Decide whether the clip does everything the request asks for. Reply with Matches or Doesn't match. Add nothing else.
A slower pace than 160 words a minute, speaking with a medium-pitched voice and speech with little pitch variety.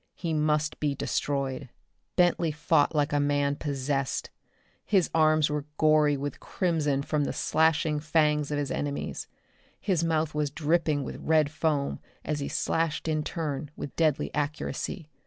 Matches